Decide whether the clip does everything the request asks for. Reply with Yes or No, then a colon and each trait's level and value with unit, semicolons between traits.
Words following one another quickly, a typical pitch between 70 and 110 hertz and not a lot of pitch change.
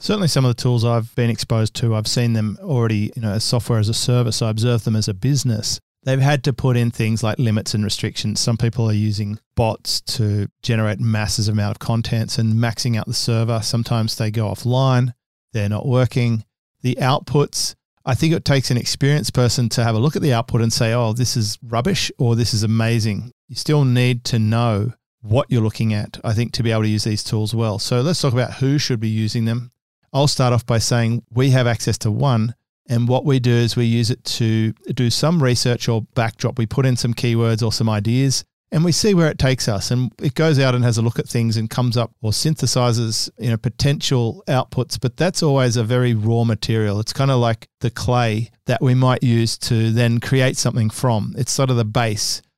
No: fast, 225 wpm; low, 120 Hz; narrow, 2.3 semitones